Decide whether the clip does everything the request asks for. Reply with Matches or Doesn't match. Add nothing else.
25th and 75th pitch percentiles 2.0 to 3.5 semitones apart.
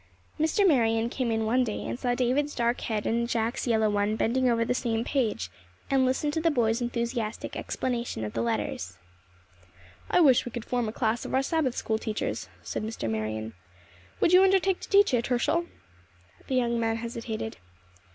Matches